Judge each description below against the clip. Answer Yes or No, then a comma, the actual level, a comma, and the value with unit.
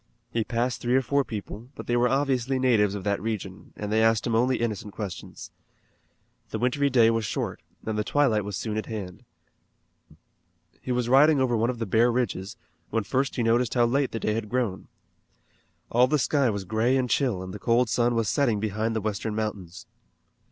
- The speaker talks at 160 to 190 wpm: No, average, 200 wpm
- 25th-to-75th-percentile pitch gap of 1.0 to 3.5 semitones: Yes, average, 2.9 semitones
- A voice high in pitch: No, low, 115 Hz